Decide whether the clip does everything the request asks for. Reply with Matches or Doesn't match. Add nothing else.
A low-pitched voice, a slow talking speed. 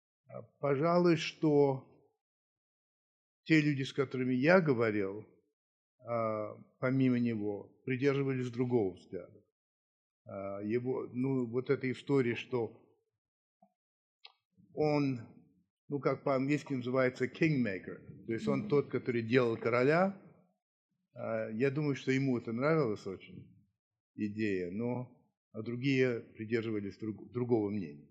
Matches